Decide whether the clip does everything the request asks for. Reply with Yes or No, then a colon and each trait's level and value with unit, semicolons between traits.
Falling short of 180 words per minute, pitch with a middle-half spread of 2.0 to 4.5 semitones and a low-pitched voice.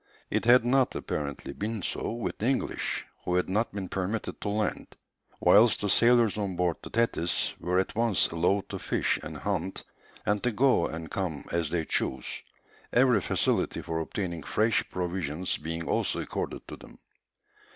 No: average, 170 wpm; average, 4.9 semitones; very low, 95 Hz